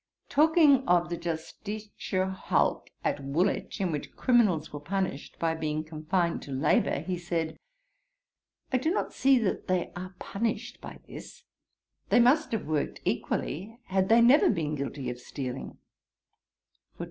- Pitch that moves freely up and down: Yes, wide, 6.3 semitones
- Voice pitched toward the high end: No, medium, 180 Hz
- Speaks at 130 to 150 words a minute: Yes, average, 145 wpm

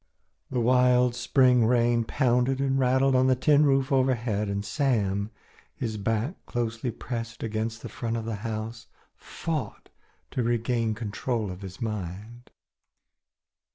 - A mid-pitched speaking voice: No, low, 120 Hz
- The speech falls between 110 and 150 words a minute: Yes, slow, 135 wpm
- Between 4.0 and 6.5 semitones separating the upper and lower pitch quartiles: No, narrow, 2.6 semitones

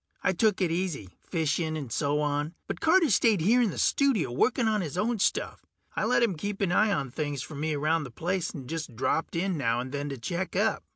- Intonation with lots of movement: Yes, wide, 5.7 semitones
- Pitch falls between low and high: Yes, medium, 165 Hz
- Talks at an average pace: No, fast, 235 wpm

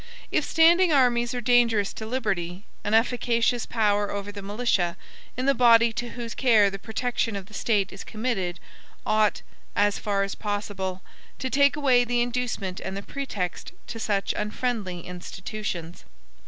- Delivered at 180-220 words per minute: No, average, 155 wpm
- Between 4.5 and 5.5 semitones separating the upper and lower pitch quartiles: No, average, 3.7 semitones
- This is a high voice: Yes, high, 215 Hz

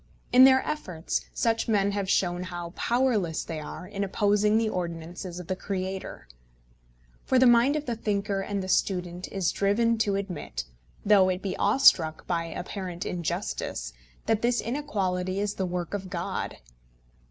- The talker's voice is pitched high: Yes, high, 195 Hz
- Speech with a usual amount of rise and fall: Yes, average, 3.5 semitones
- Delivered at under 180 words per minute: Yes, average, 160 wpm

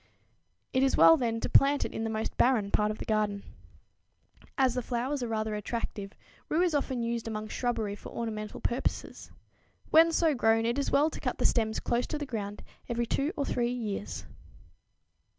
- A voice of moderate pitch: No, high, 235 Hz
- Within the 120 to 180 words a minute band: No, average, 190 wpm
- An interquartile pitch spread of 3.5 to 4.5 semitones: Yes, average, 3.8 semitones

